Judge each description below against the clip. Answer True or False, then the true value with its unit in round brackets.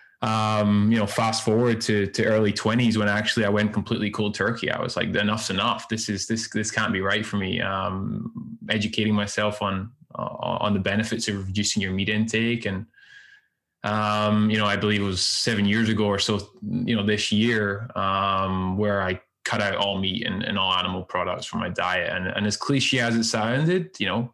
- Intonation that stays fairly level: True (1.8 semitones)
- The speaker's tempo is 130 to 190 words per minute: False (205 wpm)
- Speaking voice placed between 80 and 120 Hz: True (105 Hz)